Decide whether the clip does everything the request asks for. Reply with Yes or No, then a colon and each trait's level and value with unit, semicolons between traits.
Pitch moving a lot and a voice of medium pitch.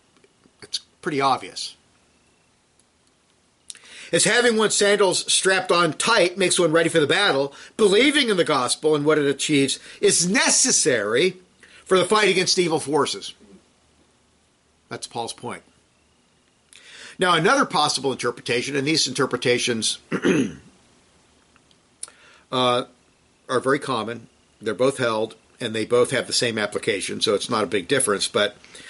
Yes: wide, 6.9 semitones; medium, 155 Hz